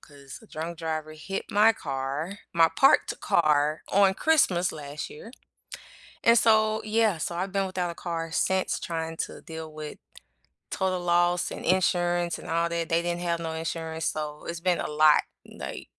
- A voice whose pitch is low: No, medium, 170 Hz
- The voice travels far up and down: No, average, 2.8 semitones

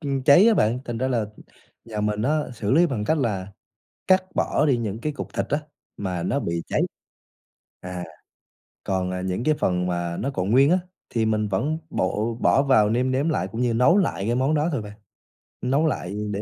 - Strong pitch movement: Yes, wide, 5.7 semitones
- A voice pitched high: No, low, 115 Hz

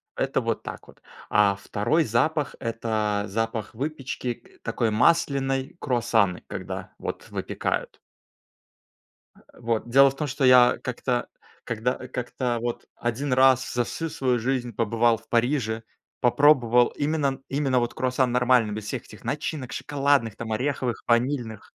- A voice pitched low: Yes, low, 125 Hz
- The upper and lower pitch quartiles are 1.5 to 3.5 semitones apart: Yes, average, 2.8 semitones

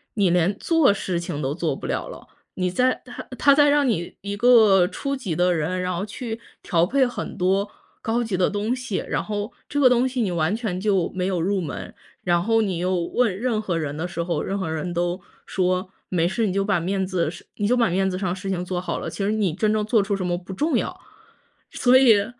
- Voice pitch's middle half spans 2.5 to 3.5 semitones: No, average, 4.0 semitones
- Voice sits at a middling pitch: No, high, 195 Hz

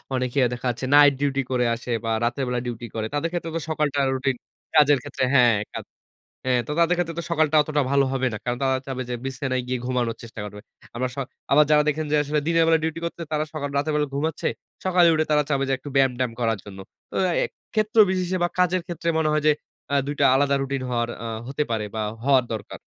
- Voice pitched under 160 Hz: Yes, medium, 140 Hz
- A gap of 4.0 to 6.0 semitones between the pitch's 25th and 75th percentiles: No, average, 3.6 semitones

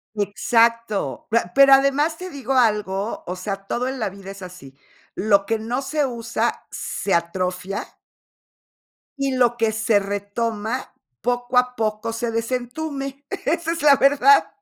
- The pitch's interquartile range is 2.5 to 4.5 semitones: No, average, 4.9 semitones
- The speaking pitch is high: Yes, high, 230 Hz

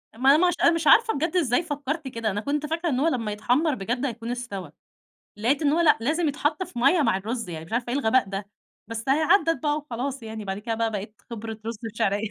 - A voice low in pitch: No, high, 245 Hz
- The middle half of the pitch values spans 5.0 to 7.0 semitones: Yes, average, 5.3 semitones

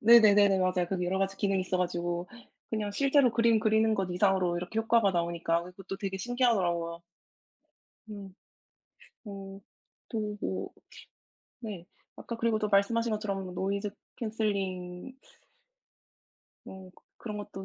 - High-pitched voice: Yes, high, 195 Hz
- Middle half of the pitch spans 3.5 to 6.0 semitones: No, average, 3.1 semitones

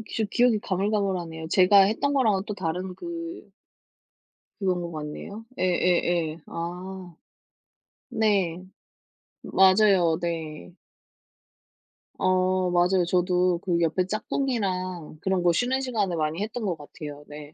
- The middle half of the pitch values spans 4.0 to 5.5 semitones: No, average, 3.2 semitones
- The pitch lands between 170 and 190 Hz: Yes, medium, 185 Hz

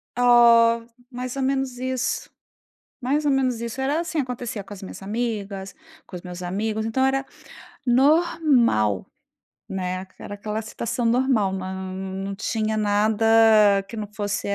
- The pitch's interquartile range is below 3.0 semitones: No, average, 4.5 semitones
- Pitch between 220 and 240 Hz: Yes, high, 230 Hz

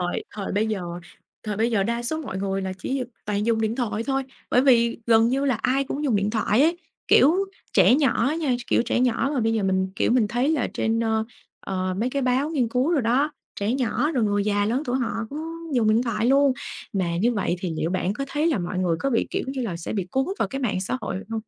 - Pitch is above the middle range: Yes, high, 230 Hz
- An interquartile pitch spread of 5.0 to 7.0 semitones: No, average, 4.6 semitones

